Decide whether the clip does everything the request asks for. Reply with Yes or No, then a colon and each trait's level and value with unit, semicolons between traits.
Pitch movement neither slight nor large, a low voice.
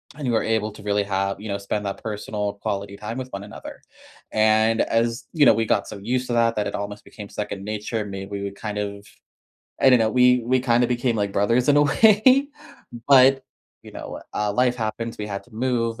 Yes: average, 3.3 semitones; low, 110 Hz